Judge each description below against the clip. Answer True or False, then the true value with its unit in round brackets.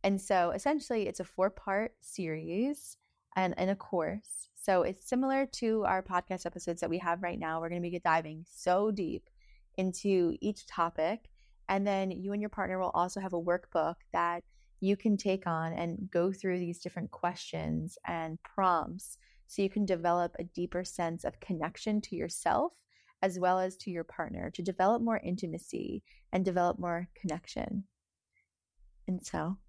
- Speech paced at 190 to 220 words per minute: False (170 wpm)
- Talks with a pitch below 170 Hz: False (185 Hz)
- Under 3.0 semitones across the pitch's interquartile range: True (2.4 semitones)